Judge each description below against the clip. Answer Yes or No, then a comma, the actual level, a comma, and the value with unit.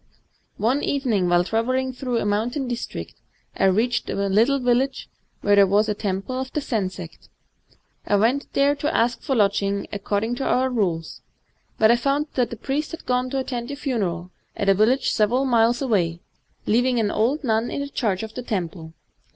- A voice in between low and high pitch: No, high, 230 Hz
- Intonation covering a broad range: No, average, 4.3 semitones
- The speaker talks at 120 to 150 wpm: No, average, 185 wpm